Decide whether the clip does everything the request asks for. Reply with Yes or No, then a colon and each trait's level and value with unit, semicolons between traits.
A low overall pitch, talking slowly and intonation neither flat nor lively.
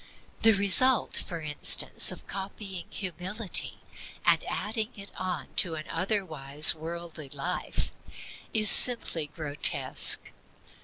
No: medium, 180 Hz; slow, 105 wpm; average, 4.5 semitones